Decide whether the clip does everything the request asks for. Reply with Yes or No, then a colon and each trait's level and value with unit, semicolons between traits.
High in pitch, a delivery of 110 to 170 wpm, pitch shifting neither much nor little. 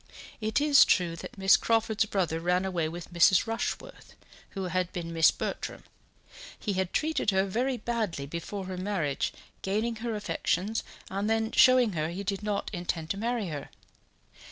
Yes: high, 195 Hz; average, 165 wpm; average, 4.1 semitones